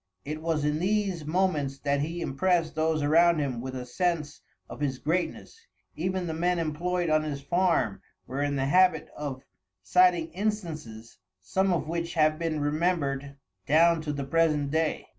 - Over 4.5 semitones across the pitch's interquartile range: No, average, 3.4 semitones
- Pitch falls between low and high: Yes, medium, 155 Hz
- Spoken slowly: No, average, 165 wpm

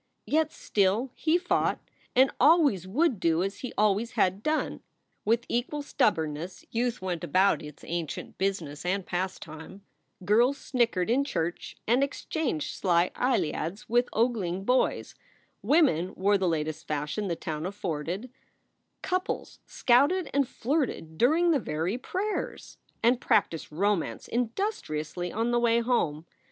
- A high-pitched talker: Yes, high, 205 Hz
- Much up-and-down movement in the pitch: Yes, wide, 6.8 semitones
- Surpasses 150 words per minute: No, slow, 135 wpm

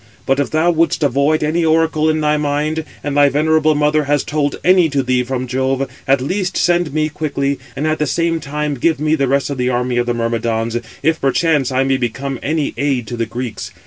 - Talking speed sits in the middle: No, fast, 220 wpm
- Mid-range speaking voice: Yes, medium, 145 Hz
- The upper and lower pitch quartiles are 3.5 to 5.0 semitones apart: No, average, 3.1 semitones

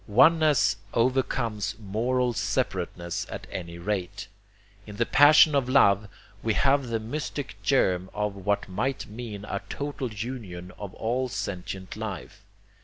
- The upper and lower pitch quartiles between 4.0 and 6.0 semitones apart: Yes, average, 4.7 semitones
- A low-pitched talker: Yes, low, 110 Hz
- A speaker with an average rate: No, slow, 130 wpm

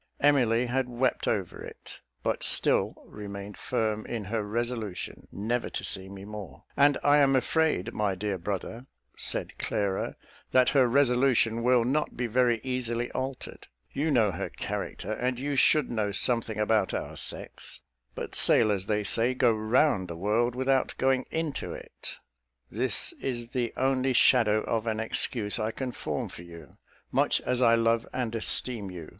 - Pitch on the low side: Yes, low, 115 Hz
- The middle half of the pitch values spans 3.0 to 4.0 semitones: Yes, average, 3.4 semitones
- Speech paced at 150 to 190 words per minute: Yes, average, 160 wpm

